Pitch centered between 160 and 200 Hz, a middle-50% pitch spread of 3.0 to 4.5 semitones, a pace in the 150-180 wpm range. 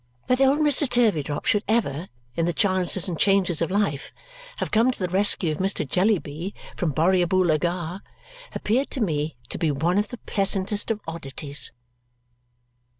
Yes: medium, 185 Hz; average, 4.2 semitones; average, 160 wpm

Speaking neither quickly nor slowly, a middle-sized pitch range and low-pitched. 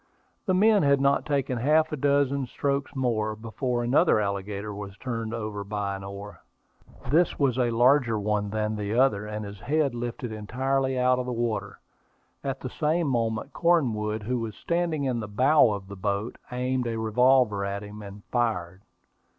Yes: average, 180 wpm; average, 4.4 semitones; low, 120 Hz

